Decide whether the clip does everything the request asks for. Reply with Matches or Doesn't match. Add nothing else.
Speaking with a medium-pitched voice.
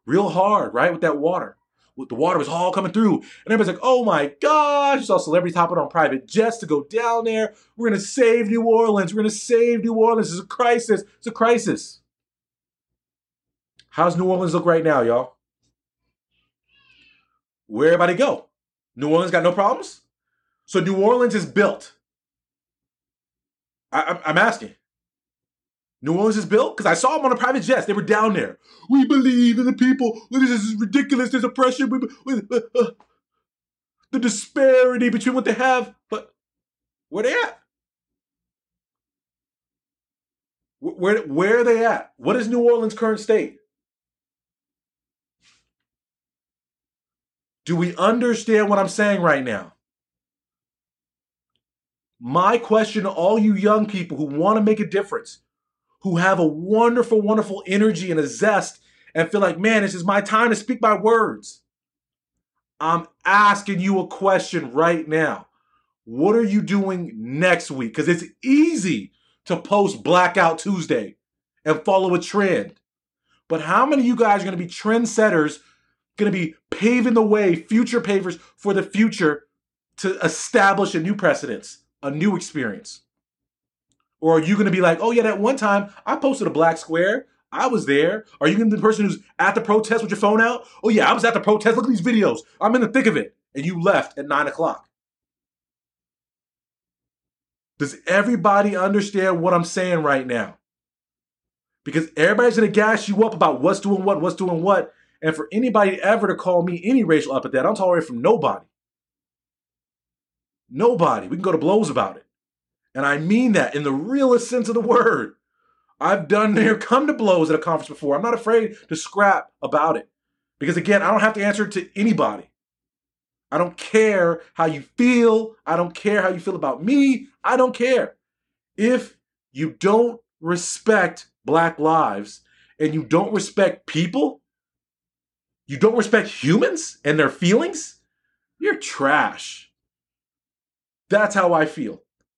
Doesn't match